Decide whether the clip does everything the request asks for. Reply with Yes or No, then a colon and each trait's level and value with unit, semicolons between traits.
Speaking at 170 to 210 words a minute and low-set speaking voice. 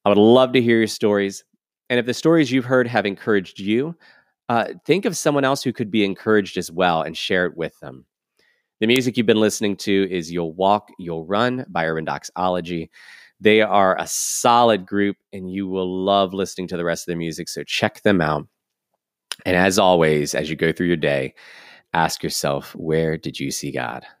Yes: fast, 205 wpm; low, 100 Hz